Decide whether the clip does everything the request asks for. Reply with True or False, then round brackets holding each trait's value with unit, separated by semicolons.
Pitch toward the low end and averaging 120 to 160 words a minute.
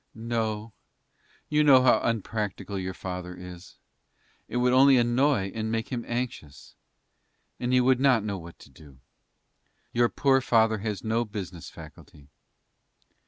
True (115 Hz; 140 wpm)